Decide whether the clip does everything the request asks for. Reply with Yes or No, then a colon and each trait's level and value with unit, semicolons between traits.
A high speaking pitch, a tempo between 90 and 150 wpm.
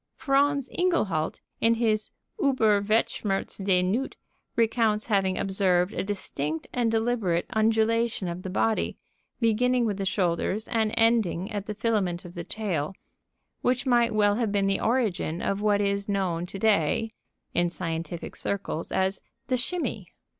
Yes: high, 205 Hz; average, 145 wpm